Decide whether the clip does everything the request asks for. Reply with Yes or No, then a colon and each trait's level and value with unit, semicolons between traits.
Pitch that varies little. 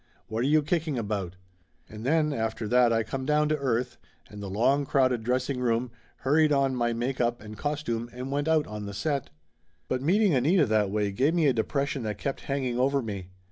No: average, 4.2 semitones